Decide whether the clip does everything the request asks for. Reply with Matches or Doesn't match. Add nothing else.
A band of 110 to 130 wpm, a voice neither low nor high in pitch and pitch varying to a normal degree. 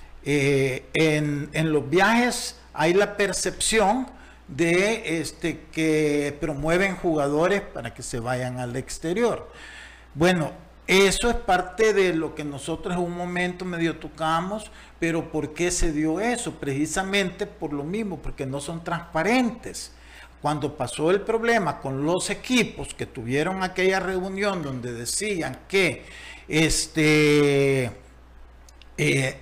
Matches